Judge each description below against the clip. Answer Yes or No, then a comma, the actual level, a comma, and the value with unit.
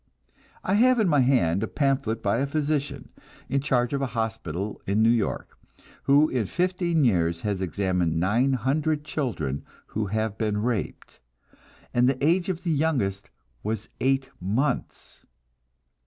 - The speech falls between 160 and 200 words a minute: No, average, 150 wpm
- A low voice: Yes, low, 125 Hz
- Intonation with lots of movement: Yes, wide, 5.9 semitones